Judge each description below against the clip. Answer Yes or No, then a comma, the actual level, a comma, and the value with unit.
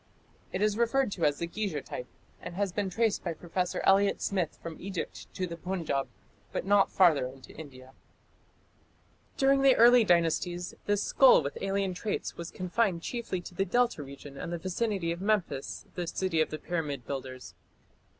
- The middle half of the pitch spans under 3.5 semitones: No, average, 4.1 semitones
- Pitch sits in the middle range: Yes, medium, 180 Hz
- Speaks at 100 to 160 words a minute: No, average, 175 wpm